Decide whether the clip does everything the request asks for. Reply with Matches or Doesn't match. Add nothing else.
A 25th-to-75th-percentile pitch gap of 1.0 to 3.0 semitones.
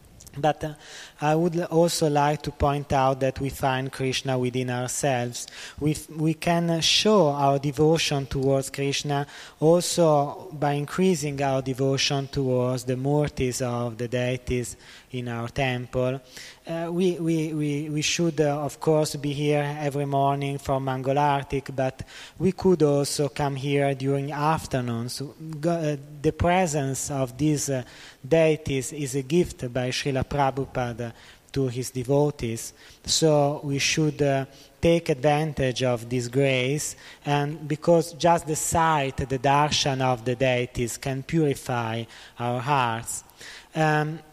Matches